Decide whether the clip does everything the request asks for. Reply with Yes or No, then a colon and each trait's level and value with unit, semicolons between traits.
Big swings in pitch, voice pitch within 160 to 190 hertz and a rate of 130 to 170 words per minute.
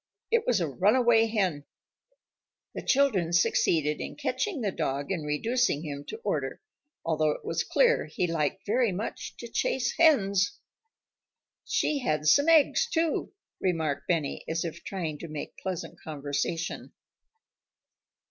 Yes: wide, 8.0 semitones; medium, 185 Hz; average, 140 wpm